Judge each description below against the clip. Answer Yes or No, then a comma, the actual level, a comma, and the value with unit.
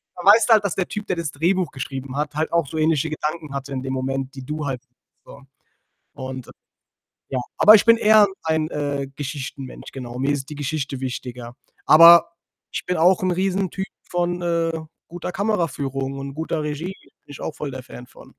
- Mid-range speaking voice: Yes, medium, 150 Hz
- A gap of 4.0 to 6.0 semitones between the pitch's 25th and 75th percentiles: Yes, average, 4.4 semitones